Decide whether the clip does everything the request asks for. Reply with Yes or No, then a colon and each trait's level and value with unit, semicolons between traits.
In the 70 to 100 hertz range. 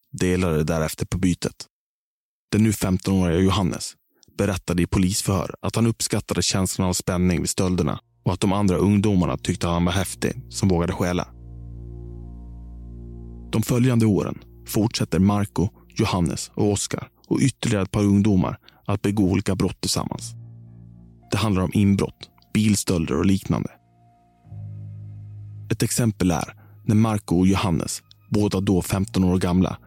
Yes: very low, 95 Hz